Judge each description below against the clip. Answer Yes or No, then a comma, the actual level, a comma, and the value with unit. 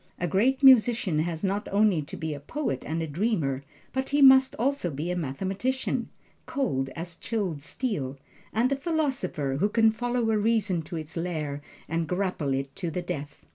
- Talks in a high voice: No, medium, 180 Hz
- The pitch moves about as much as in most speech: No, wide, 7.2 semitones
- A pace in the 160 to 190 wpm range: Yes, average, 180 wpm